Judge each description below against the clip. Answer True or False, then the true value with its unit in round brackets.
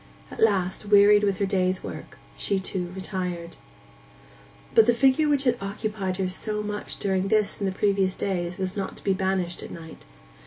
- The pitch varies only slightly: True (2.0 semitones)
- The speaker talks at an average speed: True (185 wpm)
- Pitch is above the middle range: True (195 Hz)